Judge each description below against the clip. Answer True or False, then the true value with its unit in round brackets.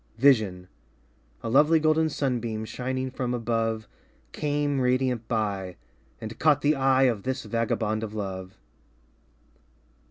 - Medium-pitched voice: False (120 Hz)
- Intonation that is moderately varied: True (3.6 semitones)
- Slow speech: True (120 wpm)